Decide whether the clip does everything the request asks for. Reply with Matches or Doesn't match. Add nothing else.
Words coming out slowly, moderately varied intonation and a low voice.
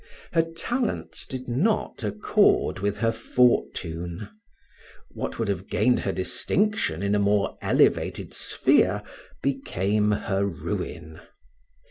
Matches